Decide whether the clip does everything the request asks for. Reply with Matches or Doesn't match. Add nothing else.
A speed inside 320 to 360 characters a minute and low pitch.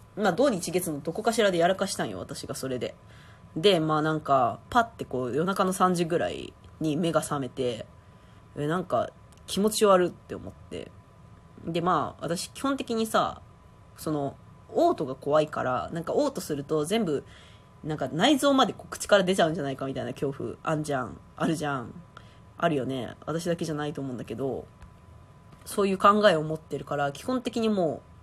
Doesn't match